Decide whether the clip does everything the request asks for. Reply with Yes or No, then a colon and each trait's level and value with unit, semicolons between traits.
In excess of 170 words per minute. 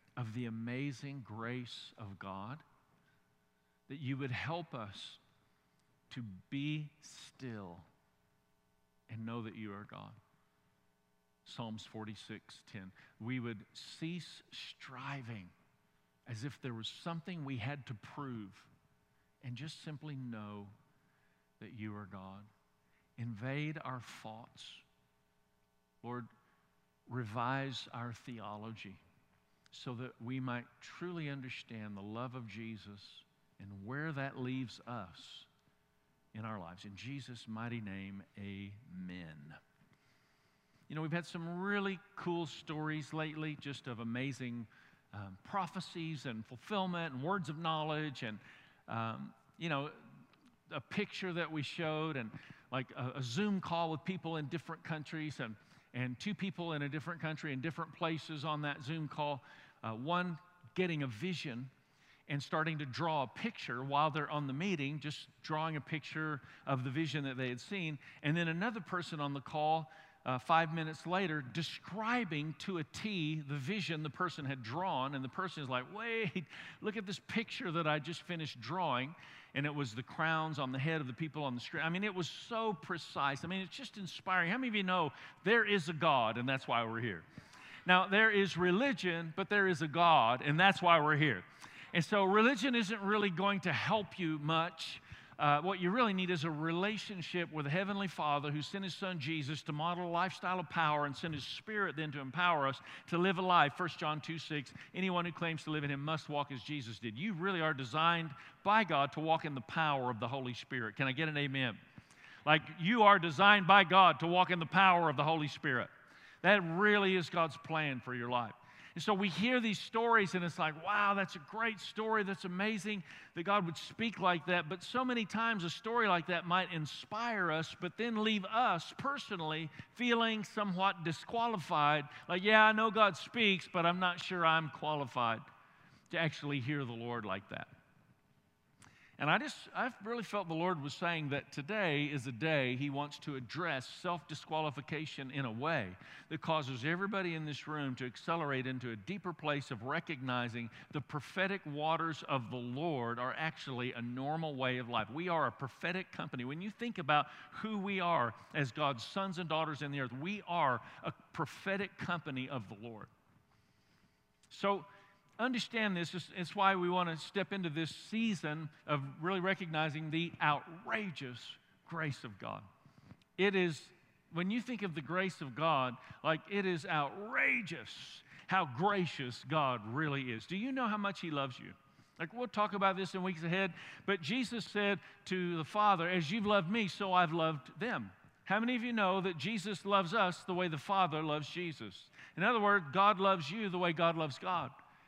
Yes: average, 180 wpm